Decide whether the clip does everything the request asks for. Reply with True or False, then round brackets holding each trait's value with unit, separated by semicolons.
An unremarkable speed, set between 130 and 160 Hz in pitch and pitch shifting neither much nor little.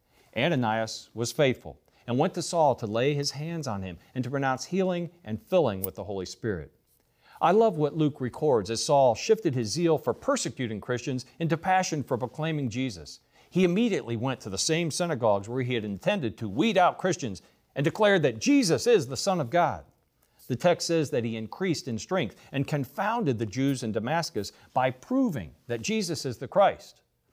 False (190 wpm; 135 Hz; 6.5 semitones)